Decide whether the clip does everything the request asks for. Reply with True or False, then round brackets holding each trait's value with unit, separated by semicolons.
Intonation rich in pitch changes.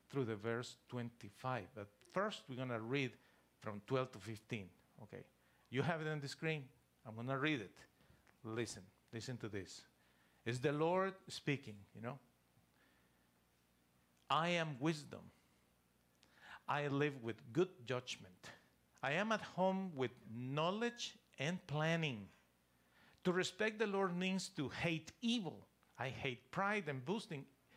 True (8.2 semitones)